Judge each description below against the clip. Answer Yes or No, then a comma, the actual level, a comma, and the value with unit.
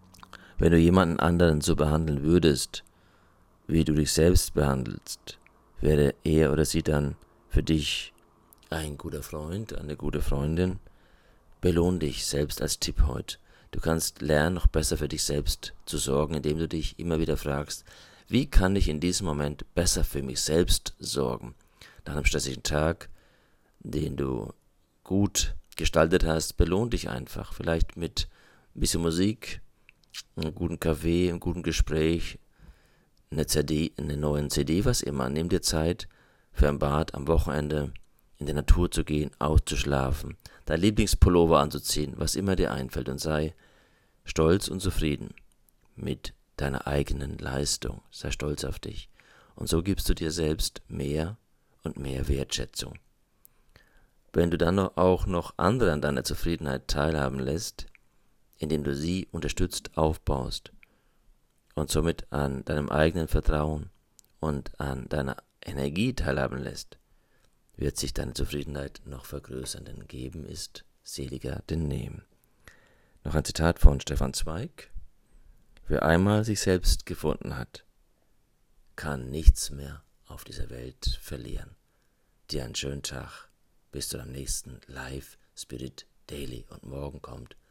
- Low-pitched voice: Yes, very low, 75 Hz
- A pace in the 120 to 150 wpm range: Yes, average, 140 wpm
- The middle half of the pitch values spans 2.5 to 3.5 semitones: Yes, average, 3.0 semitones